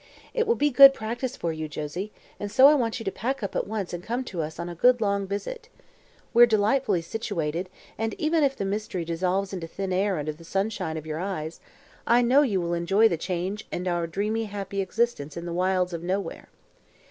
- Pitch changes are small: No, average, 4.7 semitones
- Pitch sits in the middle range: No, high, 195 Hz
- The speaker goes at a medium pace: No, fast, 220 wpm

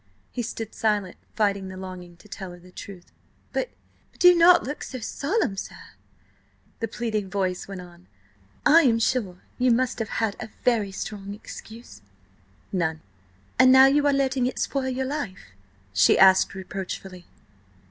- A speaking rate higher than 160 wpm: No, average, 155 wpm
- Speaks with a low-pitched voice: No, high, 215 Hz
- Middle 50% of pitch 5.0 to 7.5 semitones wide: Yes, wide, 5.4 semitones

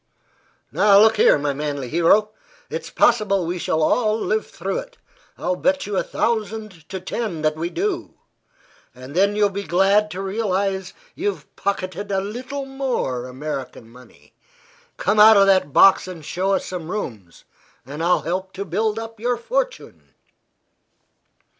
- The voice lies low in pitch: No, high, 195 Hz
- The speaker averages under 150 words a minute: No, average, 155 wpm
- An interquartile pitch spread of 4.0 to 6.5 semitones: Yes, average, 4.8 semitones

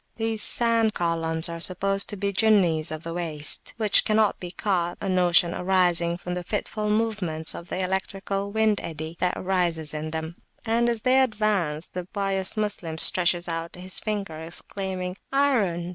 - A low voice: No, medium, 185 Hz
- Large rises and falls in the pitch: No, average, 3.8 semitones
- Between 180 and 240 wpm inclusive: No, average, 160 wpm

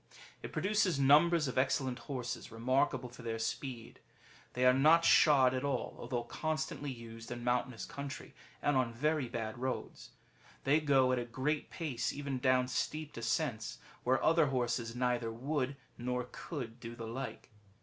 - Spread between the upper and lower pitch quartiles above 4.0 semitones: No, average, 3.3 semitones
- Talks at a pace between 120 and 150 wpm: No, average, 160 wpm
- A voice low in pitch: Yes, low, 130 Hz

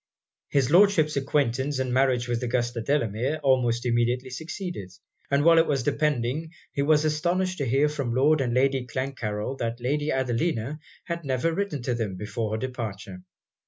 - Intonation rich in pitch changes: No, average, 4.0 semitones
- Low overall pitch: Yes, low, 130 Hz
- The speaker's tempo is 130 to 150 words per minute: No, average, 160 wpm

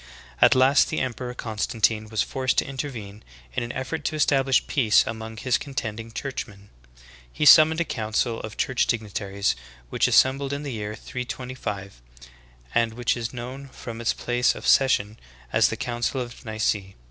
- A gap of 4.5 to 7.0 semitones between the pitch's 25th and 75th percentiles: No, average, 3.3 semitones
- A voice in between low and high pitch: No, low, 120 Hz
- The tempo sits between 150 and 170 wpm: Yes, average, 160 wpm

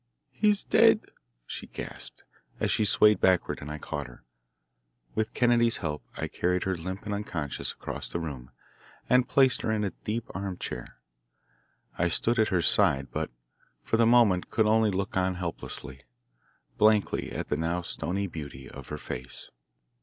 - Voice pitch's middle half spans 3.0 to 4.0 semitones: No, average, 5.2 semitones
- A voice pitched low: Yes, very low, 95 Hz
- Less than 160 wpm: No, average, 165 wpm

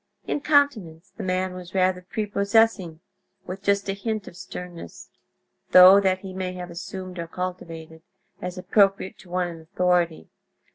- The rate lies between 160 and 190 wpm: No, average, 150 wpm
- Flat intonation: Yes, narrow, 1.8 semitones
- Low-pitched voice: No, medium, 185 Hz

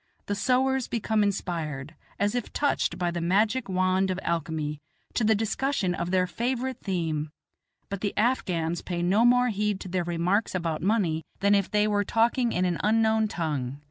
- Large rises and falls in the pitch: No, average, 4.4 semitones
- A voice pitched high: Yes, high, 195 Hz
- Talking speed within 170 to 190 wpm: Yes, average, 175 wpm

